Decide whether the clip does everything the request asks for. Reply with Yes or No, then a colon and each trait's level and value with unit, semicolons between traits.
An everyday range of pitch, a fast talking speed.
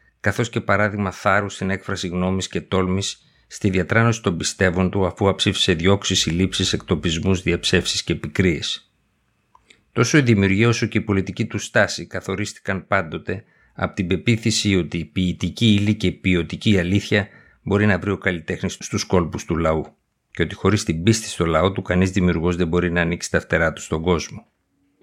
No: narrow, 2.3 semitones; fast, 175 wpm